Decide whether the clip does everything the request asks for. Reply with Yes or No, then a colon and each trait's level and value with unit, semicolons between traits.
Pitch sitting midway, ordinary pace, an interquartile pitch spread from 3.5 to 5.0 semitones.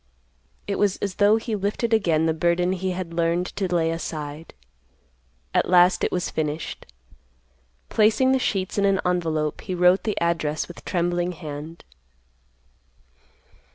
No: medium, 175 Hz; average, 145 wpm; average, 3.1 semitones